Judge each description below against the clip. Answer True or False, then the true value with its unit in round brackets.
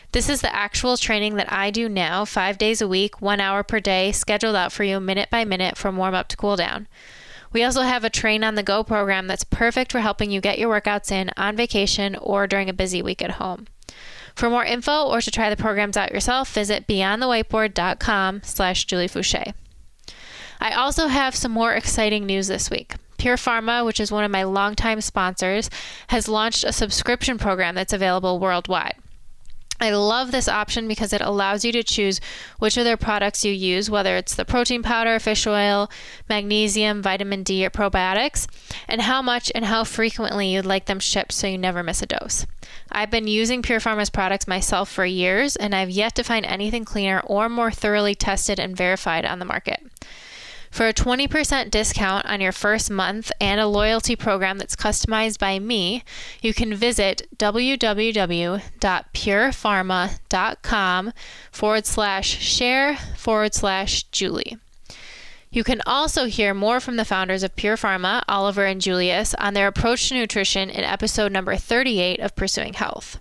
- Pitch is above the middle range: True (210 Hz)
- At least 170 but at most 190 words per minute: True (175 wpm)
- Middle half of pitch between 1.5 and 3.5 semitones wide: True (2.8 semitones)